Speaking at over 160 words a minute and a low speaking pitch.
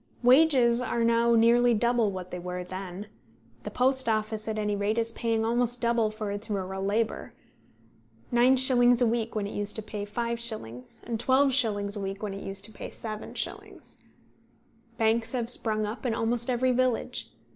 No: average, 170 wpm; high, 225 Hz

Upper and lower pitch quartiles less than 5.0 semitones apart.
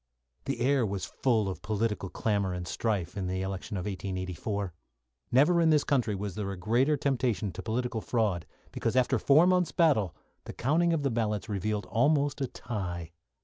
No: wide, 5.5 semitones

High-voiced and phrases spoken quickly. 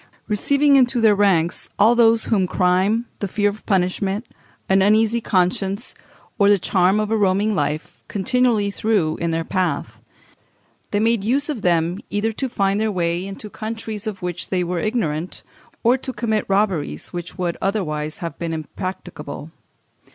No: high, 200 Hz; average, 160 wpm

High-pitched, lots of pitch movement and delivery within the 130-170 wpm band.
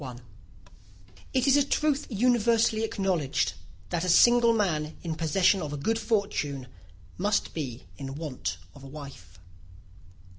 No: medium, 180 Hz; wide, 7.7 semitones; average, 140 wpm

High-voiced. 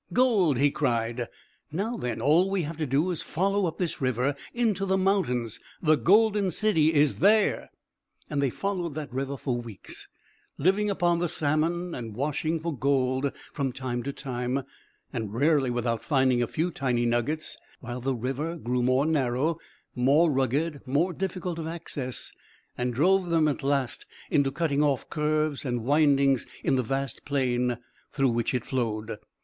No: medium, 140 Hz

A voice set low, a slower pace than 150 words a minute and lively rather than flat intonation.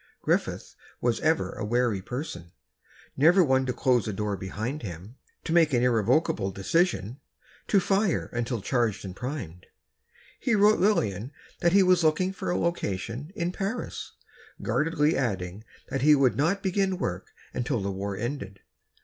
No: low, 130 Hz; average, 155 wpm; wide, 8.5 semitones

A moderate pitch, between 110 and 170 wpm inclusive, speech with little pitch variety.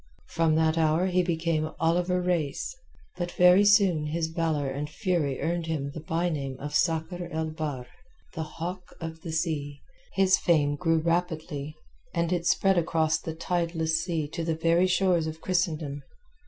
Yes: medium, 165 Hz; average, 165 wpm; narrow, 2.0 semitones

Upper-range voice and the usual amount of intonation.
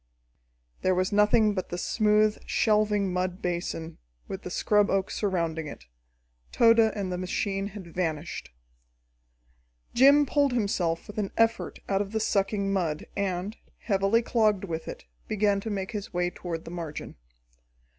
Yes: high, 195 Hz; average, 3.1 semitones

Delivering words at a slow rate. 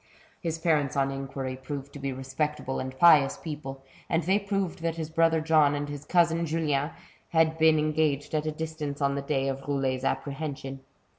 No: average, 180 wpm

